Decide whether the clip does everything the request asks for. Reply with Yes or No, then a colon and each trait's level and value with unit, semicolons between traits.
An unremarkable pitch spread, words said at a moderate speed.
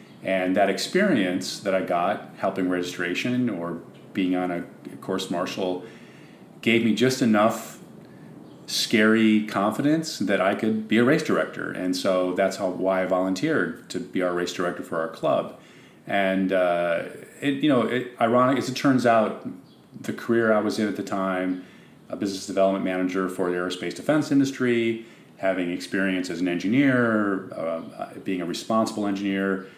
Yes: average, 3.9 semitones; average, 160 wpm